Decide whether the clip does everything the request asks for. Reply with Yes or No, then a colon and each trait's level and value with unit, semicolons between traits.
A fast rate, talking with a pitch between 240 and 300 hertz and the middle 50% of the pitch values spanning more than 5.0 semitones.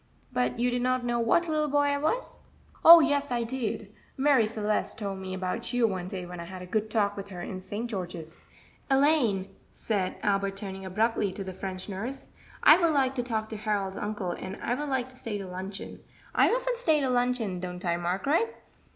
No: fast, 210 wpm; high, 215 Hz; wide, 5.5 semitones